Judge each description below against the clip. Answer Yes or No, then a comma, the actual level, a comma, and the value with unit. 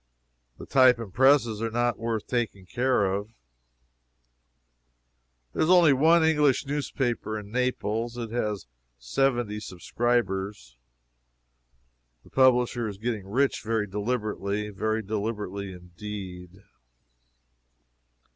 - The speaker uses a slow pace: Yes, slow, 105 wpm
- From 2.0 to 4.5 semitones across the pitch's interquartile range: Yes, average, 3.6 semitones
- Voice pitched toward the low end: Yes, low, 110 Hz